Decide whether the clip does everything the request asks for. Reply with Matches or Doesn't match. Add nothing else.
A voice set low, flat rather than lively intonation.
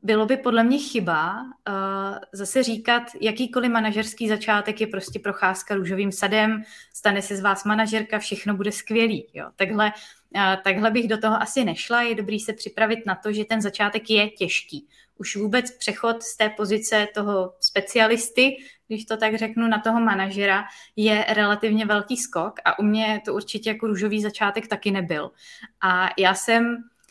Doesn't match